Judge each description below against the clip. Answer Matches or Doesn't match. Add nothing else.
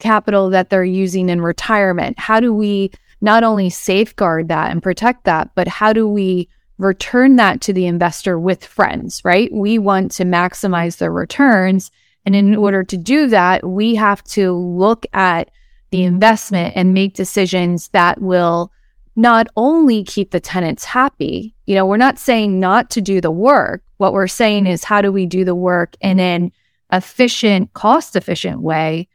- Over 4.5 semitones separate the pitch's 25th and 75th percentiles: Doesn't match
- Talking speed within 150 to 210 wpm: Matches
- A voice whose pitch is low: Doesn't match